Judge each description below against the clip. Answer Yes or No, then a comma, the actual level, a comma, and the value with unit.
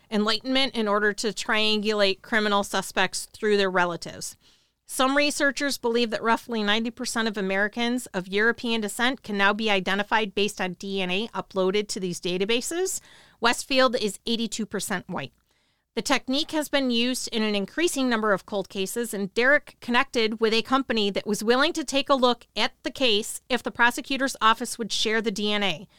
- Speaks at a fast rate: No, average, 165 wpm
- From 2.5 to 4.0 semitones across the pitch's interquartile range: Yes, average, 3.6 semitones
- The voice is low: No, high, 225 Hz